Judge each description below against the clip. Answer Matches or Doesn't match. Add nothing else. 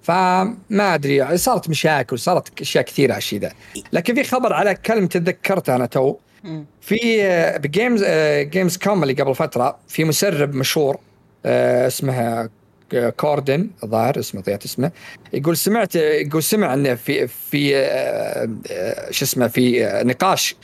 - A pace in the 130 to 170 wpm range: Matches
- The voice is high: Doesn't match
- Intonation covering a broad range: Matches